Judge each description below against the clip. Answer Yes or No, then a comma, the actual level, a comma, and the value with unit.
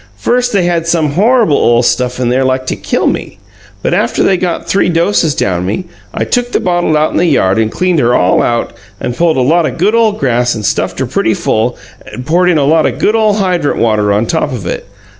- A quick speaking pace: Yes, fast, 240 wpm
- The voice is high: No, medium, 155 Hz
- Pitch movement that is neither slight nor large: No, wide, 7.0 semitones